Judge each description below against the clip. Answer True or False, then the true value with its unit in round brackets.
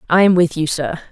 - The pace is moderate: False (270 wpm)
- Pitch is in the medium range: True (165 Hz)